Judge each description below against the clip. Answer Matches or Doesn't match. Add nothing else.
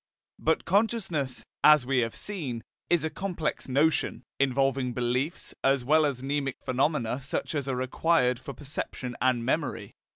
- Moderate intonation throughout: Matches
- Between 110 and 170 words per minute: Matches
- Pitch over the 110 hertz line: Matches